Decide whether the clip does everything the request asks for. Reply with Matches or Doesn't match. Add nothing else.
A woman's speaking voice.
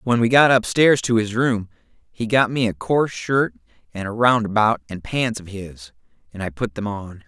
Doesn't match